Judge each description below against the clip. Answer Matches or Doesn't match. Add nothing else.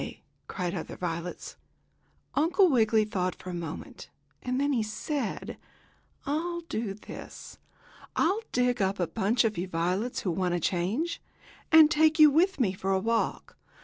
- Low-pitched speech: Doesn't match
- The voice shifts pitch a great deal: Matches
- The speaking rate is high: Doesn't match